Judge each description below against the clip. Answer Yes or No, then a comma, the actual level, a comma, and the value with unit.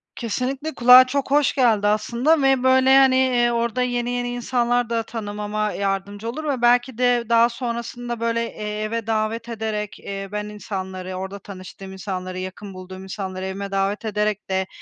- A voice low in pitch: No, high, 225 Hz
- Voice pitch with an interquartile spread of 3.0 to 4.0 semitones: Yes, average, 3.5 semitones